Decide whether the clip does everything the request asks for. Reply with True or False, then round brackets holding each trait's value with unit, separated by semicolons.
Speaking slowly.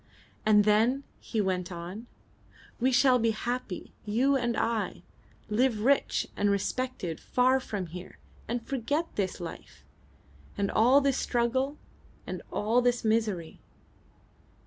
True (125 wpm)